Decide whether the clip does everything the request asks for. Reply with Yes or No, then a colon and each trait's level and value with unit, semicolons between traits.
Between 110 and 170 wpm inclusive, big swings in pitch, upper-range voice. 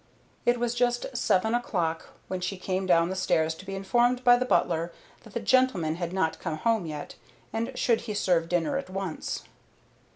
No: average, 190 wpm; wide, 6.0 semitones; high, 195 Hz